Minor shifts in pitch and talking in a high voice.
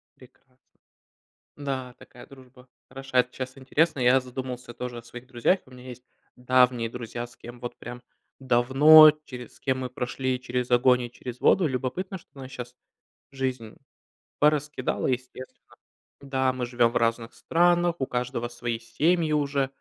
No: narrow, 1.6 semitones; low, 125 Hz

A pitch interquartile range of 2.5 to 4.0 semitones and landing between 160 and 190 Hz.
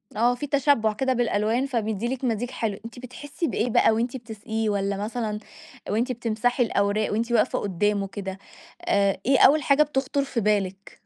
No: average, 3.4 semitones; high, 225 Hz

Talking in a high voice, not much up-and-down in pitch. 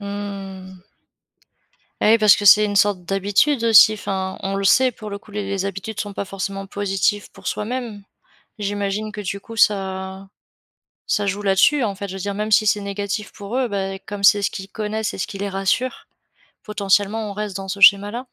Yes: high, 200 Hz; narrow, 1.4 semitones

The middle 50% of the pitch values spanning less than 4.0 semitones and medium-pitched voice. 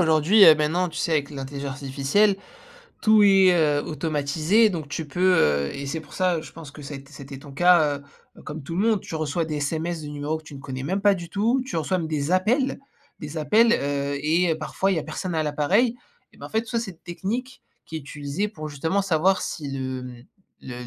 No: average, 4.5 semitones; medium, 160 Hz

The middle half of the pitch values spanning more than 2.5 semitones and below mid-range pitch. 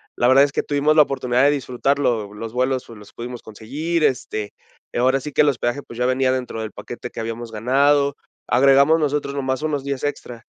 Yes: average, 2.9 semitones; low, 130 Hz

